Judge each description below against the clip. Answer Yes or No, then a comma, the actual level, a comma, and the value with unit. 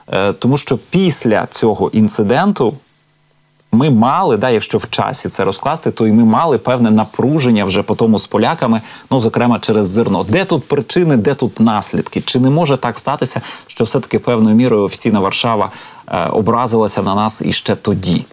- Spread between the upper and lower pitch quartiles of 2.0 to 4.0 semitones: Yes, average, 3.4 semitones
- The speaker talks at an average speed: No, fast, 170 wpm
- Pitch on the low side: Yes, low, 115 Hz